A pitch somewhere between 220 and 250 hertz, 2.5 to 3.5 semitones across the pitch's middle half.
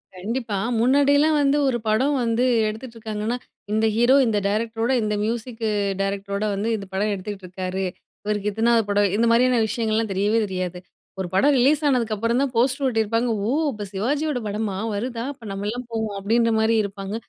Yes: high, 225 Hz; average, 3.0 semitones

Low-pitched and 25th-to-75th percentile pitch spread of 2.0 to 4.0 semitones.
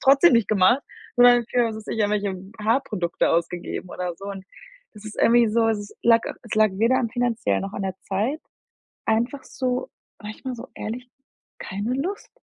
No: high, 225 Hz; average, 3.4 semitones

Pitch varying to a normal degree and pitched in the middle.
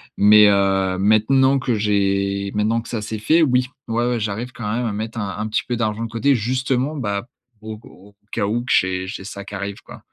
No: average, 3.2 semitones; low, 110 Hz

